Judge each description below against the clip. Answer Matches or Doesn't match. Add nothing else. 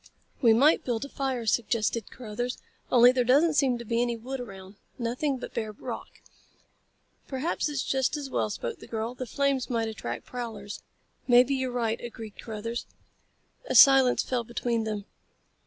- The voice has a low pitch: Doesn't match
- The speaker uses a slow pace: Doesn't match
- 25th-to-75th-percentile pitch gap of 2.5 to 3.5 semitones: Matches